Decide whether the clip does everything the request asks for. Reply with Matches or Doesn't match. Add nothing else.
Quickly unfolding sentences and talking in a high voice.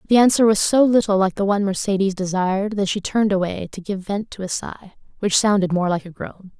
Matches